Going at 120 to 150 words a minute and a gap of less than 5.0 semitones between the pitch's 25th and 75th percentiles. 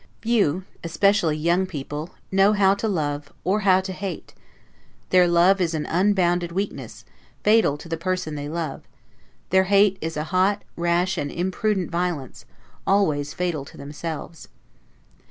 Yes: average, 145 wpm; average, 3.4 semitones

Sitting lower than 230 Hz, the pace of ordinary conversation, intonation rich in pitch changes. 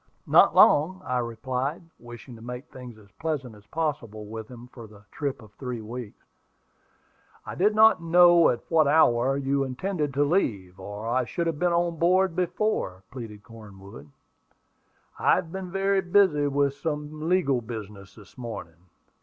Yes: low, 135 Hz; average, 160 wpm; wide, 6.7 semitones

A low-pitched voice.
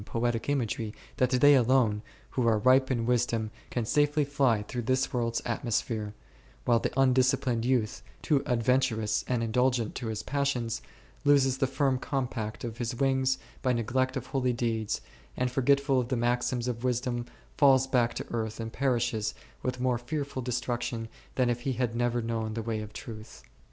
Yes: low, 120 Hz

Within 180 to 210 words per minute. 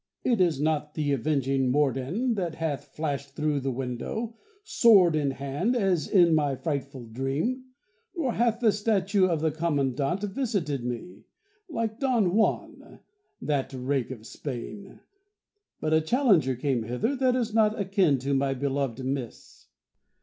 No: average, 145 wpm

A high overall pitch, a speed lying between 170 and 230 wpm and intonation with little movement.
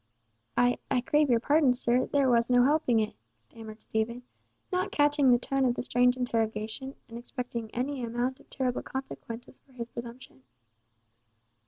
No: high, 245 Hz; average, 155 wpm; narrow, 2.3 semitones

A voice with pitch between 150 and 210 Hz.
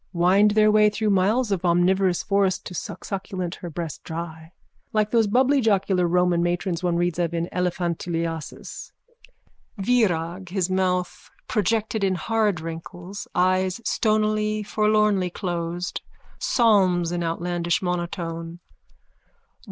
Yes: medium, 185 Hz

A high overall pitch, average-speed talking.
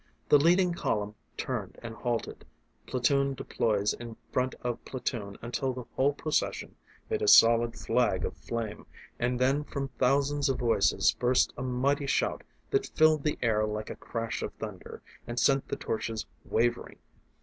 No: low, 125 Hz; average, 160 wpm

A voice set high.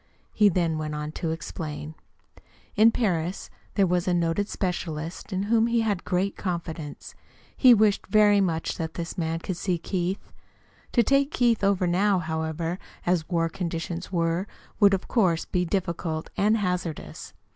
No: medium, 180 Hz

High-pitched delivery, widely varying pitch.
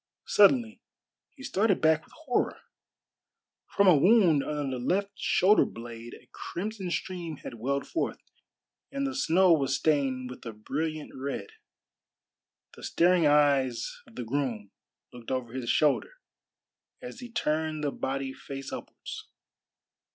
No: medium, 150 Hz; wide, 6.4 semitones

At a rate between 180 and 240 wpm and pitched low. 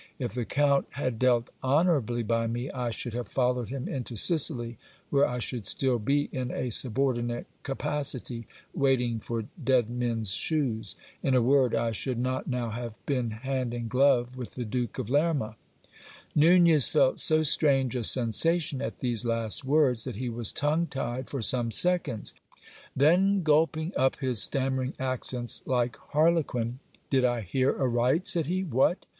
No: average, 165 wpm; low, 130 Hz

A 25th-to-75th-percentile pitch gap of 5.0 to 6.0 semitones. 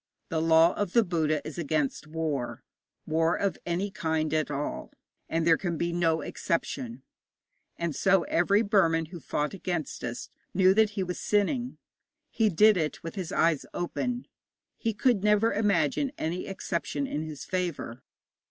No: average, 4.1 semitones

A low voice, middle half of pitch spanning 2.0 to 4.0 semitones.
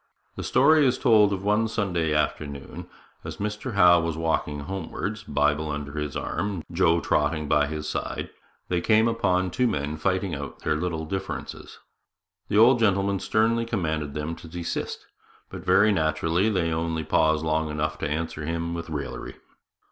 No: very low, 85 Hz; average, 4.6 semitones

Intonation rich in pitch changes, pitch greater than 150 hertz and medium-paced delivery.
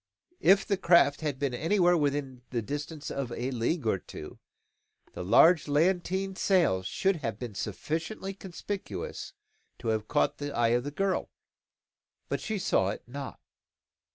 No: wide, 7.0 semitones; medium, 145 Hz; average, 155 wpm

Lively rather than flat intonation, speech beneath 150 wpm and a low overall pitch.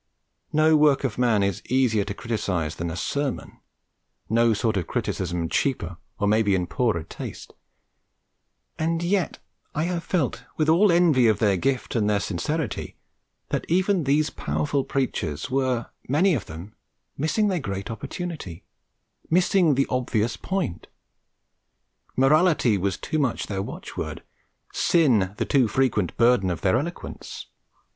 Yes: wide, 7.5 semitones; average, 140 wpm; low, 125 Hz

